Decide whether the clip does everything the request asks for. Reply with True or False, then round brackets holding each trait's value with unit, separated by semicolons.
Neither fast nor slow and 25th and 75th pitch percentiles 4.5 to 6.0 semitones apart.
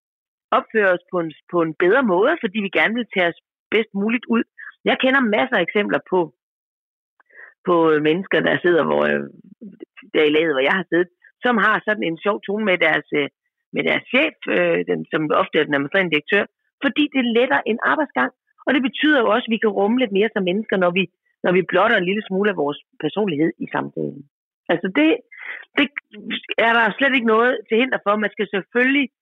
True (205 wpm; 5.1 semitones)